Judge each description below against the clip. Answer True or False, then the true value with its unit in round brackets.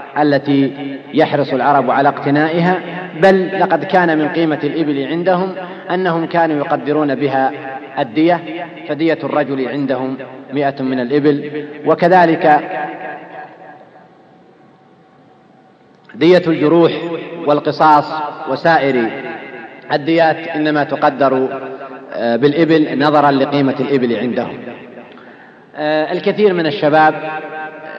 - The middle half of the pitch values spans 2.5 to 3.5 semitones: True (2.8 semitones)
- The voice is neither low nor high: True (150 Hz)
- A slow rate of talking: False (85 wpm)